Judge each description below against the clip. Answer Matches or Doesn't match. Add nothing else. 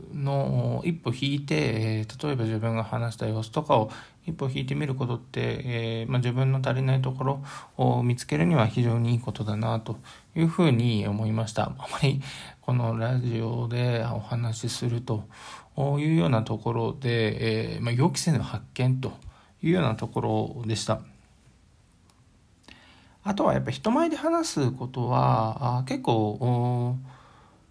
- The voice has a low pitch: Matches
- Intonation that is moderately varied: Matches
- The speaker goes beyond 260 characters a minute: Matches